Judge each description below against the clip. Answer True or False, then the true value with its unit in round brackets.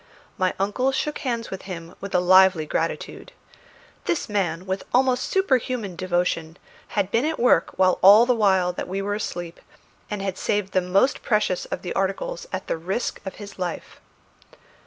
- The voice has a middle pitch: False (195 Hz)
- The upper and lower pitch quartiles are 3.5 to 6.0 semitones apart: True (4.3 semitones)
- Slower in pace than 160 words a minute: False (170 wpm)